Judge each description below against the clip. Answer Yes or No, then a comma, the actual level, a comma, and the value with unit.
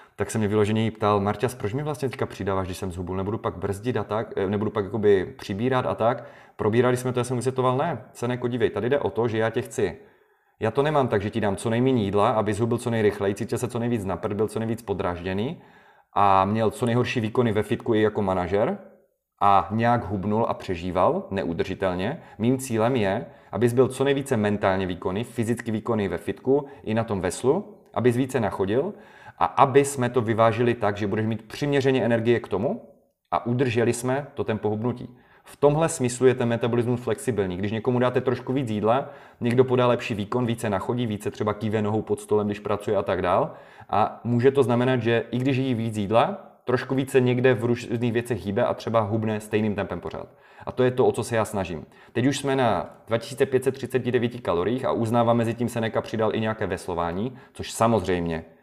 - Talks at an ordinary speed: No, fast, 205 wpm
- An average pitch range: Yes, average, 3.1 semitones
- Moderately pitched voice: No, low, 115 Hz